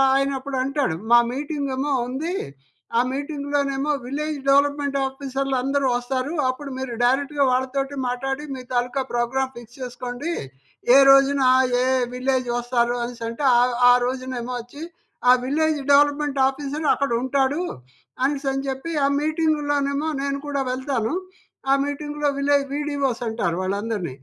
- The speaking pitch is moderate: No, very high, 275 Hz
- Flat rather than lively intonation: Yes, narrow, 2.2 semitones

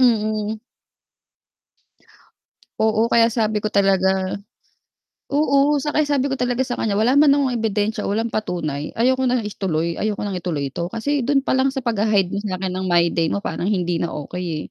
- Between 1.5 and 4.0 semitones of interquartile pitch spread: No, average, 5.2 semitones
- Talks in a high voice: Yes, high, 215 Hz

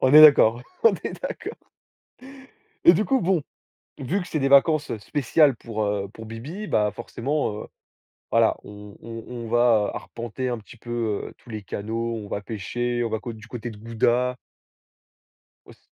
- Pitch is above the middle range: No, low, 120 Hz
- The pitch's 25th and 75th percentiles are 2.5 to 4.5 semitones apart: Yes, average, 3.9 semitones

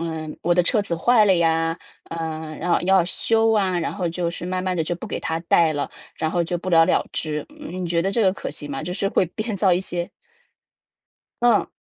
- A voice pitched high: No, medium, 175 Hz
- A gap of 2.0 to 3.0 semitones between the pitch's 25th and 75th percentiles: Yes, narrow, 2.6 semitones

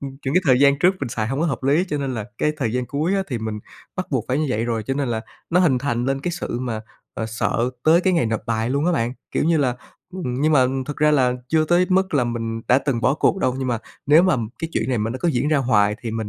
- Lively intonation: No, average, 4.8 semitones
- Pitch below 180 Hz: Yes, low, 135 Hz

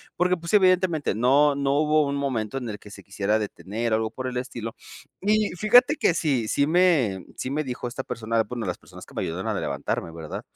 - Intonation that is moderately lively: No, wide, 6.3 semitones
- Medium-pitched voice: No, low, 130 Hz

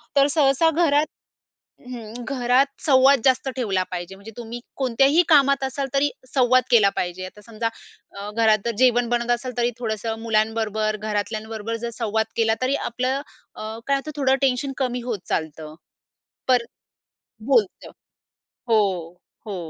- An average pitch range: Yes, average, 3.5 semitones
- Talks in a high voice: Yes, high, 240 Hz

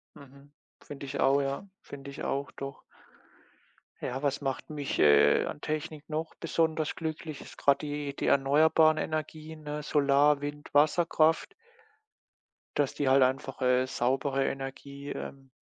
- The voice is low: No, medium, 145 Hz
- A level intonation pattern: Yes, narrow, 2.1 semitones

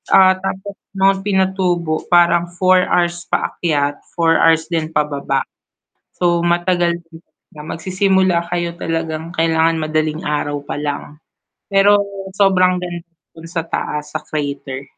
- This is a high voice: No, medium, 170 Hz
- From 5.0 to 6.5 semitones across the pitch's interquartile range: No, average, 2.8 semitones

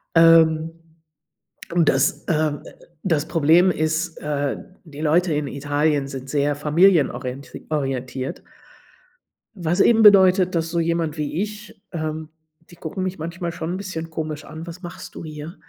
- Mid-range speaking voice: Yes, medium, 160 Hz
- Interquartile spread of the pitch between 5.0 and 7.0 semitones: No, average, 2.8 semitones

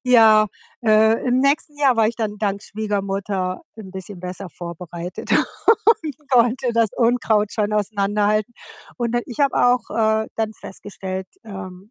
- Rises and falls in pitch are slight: No, average, 3.3 semitones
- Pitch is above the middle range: Yes, high, 215 Hz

